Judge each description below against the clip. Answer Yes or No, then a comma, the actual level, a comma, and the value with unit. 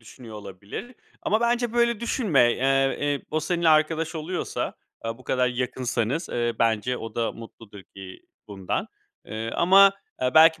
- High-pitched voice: No, low, 130 Hz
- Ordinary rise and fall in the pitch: No, wide, 7.0 semitones